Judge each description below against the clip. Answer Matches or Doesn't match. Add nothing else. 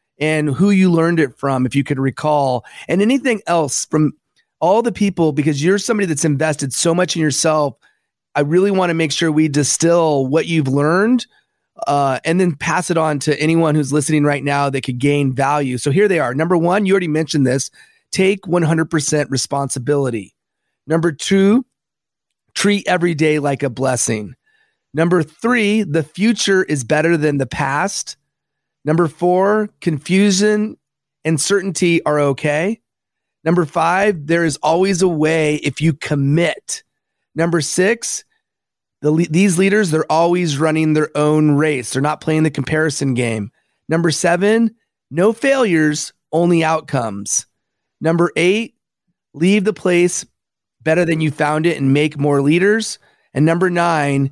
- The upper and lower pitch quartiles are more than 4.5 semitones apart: Doesn't match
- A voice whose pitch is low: Doesn't match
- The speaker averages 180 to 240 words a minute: Doesn't match